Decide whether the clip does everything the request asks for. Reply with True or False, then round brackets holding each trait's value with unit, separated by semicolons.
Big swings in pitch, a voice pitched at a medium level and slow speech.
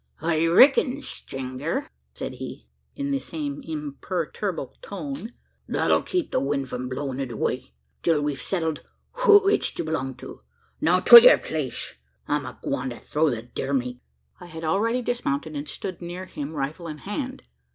False (6.3 semitones; 160 Hz; 160 wpm)